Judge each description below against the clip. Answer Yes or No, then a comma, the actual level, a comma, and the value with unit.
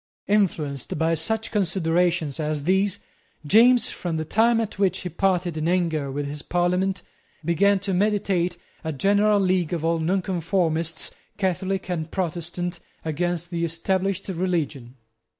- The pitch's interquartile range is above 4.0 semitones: No, average, 3.1 semitones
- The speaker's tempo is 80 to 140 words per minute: Yes, slow, 135 wpm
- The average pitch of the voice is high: No, medium, 175 Hz